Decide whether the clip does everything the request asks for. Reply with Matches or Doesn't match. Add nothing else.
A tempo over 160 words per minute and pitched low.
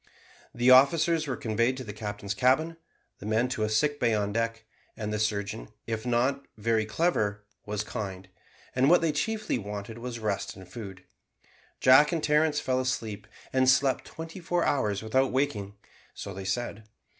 Matches